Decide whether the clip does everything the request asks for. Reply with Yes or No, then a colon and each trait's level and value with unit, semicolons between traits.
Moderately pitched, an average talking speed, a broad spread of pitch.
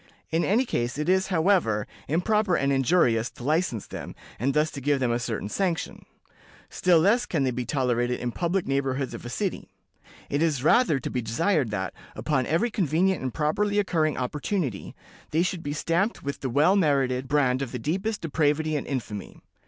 Yes: medium, 150 Hz; average, 190 wpm; wide, 5.8 semitones